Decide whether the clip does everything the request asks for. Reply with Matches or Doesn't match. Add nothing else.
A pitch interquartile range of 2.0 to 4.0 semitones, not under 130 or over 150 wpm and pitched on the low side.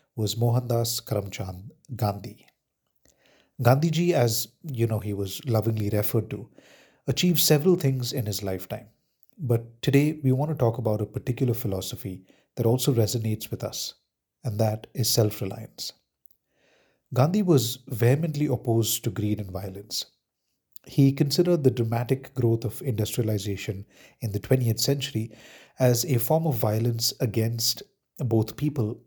Matches